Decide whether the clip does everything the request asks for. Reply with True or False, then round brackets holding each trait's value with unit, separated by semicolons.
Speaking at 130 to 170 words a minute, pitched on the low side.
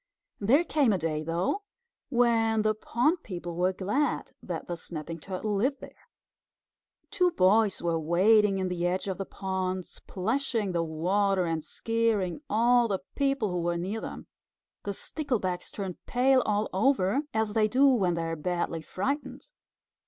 False (160 wpm; 200 Hz)